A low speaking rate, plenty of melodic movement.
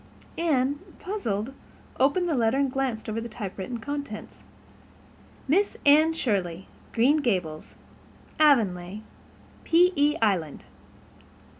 Yes: slow, 100 wpm; wide, 6.0 semitones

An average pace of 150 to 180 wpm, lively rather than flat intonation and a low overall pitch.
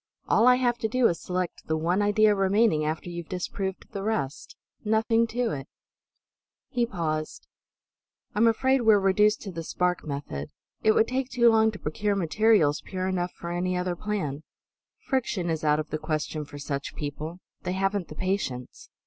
No: average, 175 wpm; wide, 5.7 semitones; medium, 185 Hz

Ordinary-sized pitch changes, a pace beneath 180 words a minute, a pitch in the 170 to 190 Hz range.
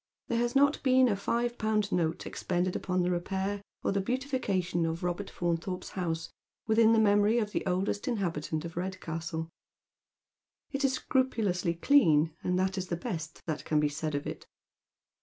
Yes: average, 4.7 semitones; average, 170 wpm; medium, 185 Hz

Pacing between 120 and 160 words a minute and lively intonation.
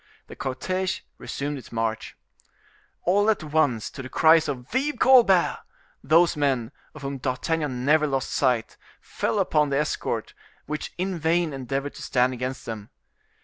No: average, 145 wpm; average, 4.6 semitones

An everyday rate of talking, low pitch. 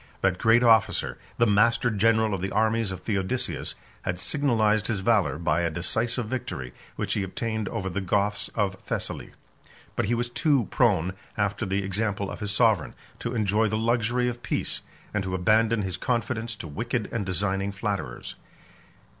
Yes: average, 170 wpm; low, 105 Hz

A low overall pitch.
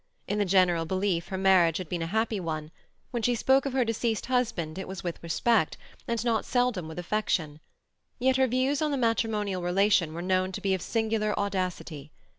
No: high, 195 Hz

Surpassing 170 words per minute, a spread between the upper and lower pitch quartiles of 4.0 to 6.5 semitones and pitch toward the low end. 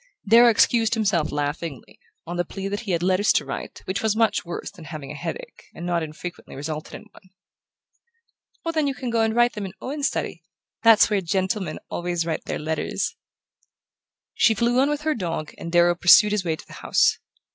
No: average, 200 wpm; average, 5.1 semitones; high, 190 Hz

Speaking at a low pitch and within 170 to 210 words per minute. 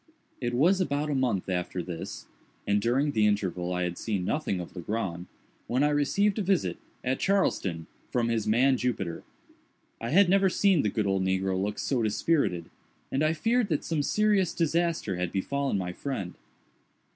Yes: low, 120 Hz; average, 175 wpm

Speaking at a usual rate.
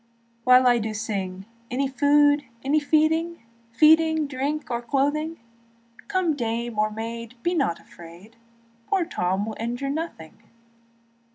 No: slow, 125 wpm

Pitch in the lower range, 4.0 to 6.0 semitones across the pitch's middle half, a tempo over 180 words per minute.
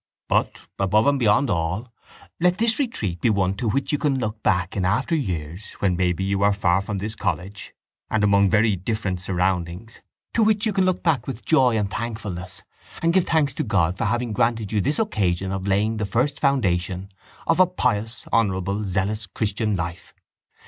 Yes: low, 105 Hz; average, 4.8 semitones; average, 190 wpm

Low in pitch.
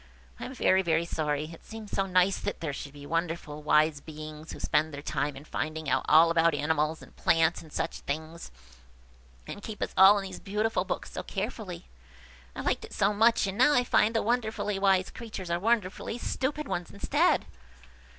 No: medium, 170 Hz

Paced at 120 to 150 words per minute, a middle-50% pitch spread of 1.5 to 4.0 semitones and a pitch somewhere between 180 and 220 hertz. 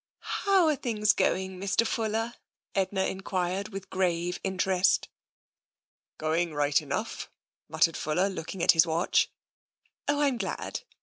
Yes: average, 140 wpm; average, 3.6 semitones; high, 190 Hz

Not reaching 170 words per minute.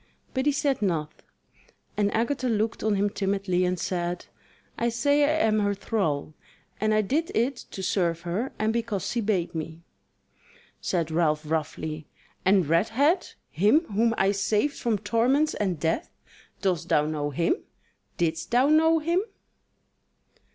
Yes: average, 150 wpm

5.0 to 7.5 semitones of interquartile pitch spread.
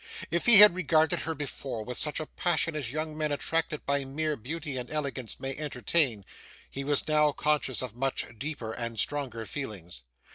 No: average, 3.7 semitones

